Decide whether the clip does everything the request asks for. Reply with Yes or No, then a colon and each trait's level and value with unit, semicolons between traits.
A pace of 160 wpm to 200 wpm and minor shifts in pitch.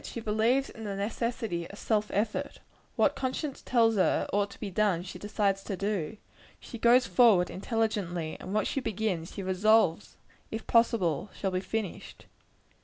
No: average, 165 wpm; average, 3.0 semitones